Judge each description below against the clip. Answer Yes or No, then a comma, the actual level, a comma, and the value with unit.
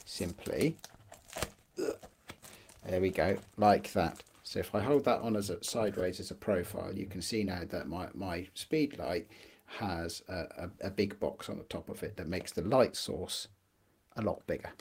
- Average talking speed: Yes, average, 185 wpm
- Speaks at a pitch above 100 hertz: No, very low, 95 Hz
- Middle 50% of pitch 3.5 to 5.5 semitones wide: No, narrow, 2.4 semitones